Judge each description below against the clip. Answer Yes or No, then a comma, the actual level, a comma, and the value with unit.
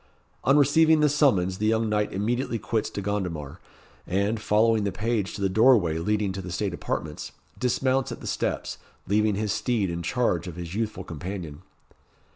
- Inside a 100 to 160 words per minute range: No, average, 175 wpm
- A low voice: Yes, low, 105 Hz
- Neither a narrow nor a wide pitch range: Yes, average, 3.9 semitones